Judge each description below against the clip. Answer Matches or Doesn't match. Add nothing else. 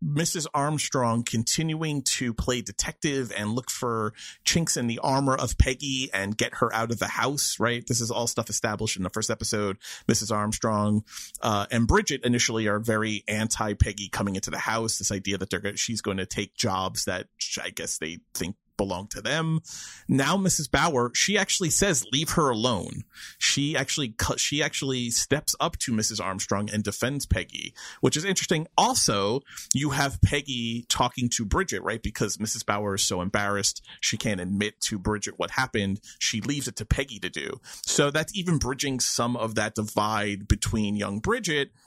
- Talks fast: Doesn't match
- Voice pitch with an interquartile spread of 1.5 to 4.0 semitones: Doesn't match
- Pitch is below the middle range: Matches